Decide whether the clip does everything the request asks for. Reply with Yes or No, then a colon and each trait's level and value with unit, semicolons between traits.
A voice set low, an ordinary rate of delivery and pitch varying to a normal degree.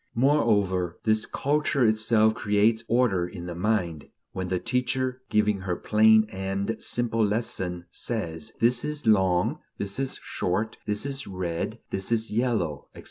Yes: low, 110 Hz; average, 145 wpm; average, 3.9 semitones